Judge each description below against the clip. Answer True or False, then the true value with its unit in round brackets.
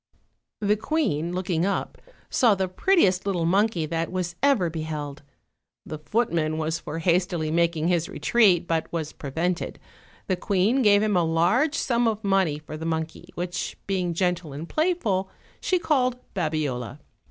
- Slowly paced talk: False (155 wpm)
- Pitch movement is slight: False (4.1 semitones)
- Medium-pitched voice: True (175 Hz)